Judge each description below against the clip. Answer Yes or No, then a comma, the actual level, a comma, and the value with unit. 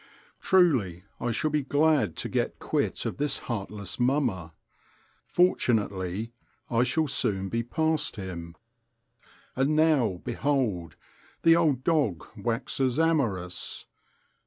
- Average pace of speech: No, slow, 110 wpm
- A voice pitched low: Yes, low, 120 Hz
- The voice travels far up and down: Yes, wide, 7.4 semitones